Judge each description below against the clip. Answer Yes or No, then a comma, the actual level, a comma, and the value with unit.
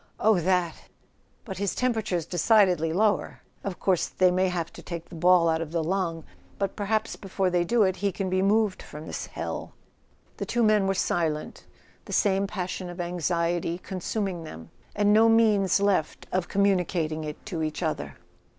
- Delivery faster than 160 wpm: Yes, average, 180 wpm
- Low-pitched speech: No, medium, 185 Hz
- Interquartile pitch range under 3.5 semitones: Yes, average, 3.0 semitones